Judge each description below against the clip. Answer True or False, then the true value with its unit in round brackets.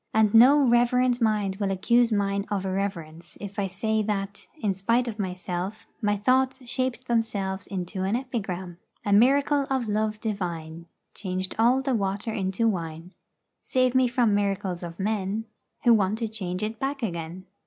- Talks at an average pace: True (165 wpm)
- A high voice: True (205 Hz)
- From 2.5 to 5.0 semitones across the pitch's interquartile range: True (3.9 semitones)